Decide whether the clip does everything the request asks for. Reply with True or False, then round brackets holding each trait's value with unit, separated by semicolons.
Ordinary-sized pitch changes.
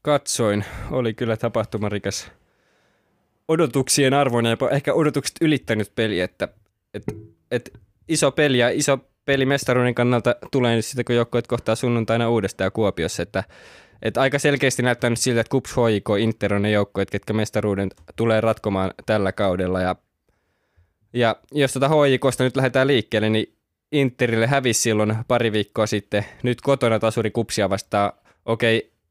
True (3.7 semitones)